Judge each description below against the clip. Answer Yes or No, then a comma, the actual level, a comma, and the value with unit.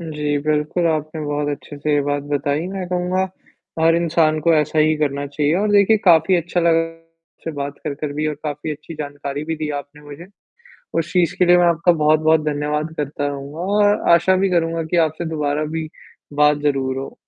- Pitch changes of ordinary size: No, narrow, 2.3 semitones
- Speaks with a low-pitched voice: No, medium, 155 Hz